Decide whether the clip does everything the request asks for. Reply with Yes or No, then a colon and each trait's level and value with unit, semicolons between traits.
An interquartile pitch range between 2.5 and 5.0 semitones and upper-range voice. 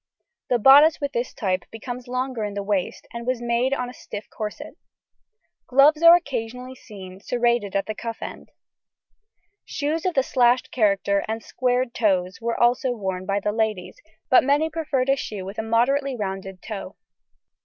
Yes: average, 4.0 semitones; high, 235 Hz